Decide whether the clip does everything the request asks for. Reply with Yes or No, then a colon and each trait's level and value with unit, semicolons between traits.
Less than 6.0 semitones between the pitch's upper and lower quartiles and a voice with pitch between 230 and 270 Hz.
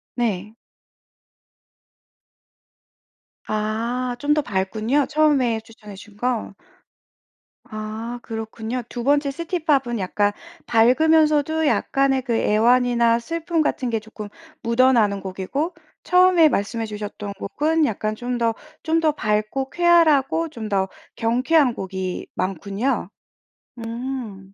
Yes: average, 5.1 semitones; high, 240 Hz